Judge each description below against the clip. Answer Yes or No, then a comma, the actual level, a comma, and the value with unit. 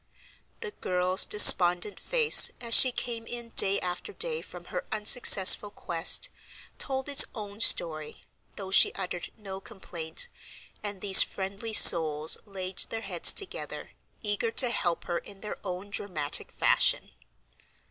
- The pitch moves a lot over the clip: No, average, 4.2 semitones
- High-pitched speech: Yes, high, 200 Hz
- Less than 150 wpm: Yes, slow, 135 wpm